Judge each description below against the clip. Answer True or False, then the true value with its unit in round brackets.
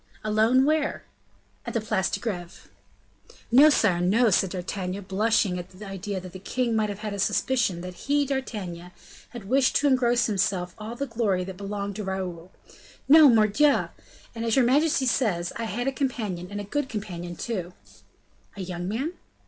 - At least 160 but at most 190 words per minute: True (180 wpm)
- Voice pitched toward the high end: True (210 Hz)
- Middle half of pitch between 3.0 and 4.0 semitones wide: False (4.7 semitones)